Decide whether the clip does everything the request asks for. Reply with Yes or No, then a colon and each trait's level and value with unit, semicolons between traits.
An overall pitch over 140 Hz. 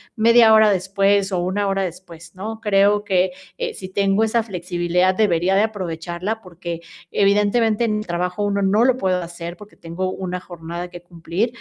Yes: high, 190 Hz